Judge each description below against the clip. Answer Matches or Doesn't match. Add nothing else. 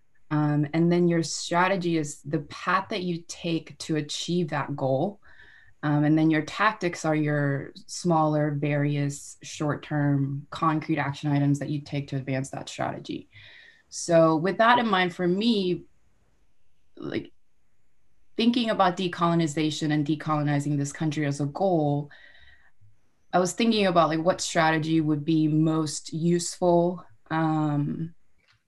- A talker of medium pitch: Matches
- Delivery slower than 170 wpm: Matches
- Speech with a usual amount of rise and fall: Matches